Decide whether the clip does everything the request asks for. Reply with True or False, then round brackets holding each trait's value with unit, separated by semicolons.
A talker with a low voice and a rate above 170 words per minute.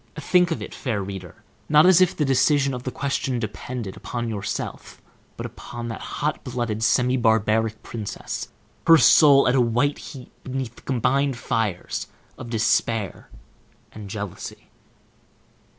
False (120 Hz; 145 wpm)